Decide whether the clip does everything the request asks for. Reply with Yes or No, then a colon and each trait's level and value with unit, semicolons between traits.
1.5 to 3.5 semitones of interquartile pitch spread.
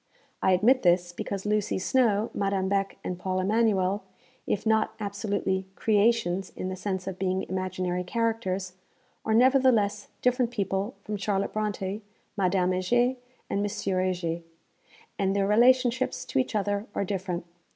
Yes: average, 2.7 semitones